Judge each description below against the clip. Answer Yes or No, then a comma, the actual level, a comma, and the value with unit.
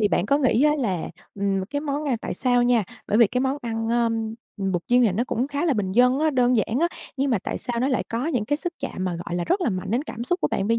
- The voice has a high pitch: Yes, high, 240 Hz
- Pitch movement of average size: Yes, average, 4.7 semitones